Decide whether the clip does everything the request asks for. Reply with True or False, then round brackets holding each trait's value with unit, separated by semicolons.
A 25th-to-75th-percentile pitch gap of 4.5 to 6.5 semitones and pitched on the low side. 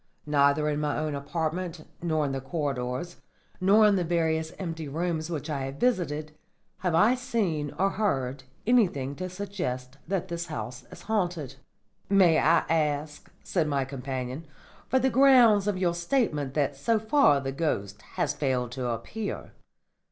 False (5.1 semitones; 160 Hz)